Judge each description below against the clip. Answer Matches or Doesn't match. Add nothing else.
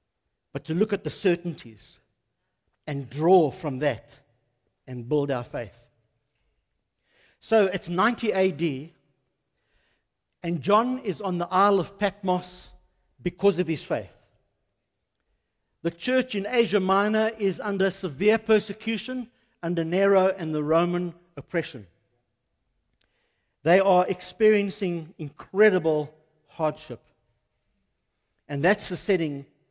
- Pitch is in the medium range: Matches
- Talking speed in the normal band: Doesn't match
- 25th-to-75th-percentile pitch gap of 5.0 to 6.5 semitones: Doesn't match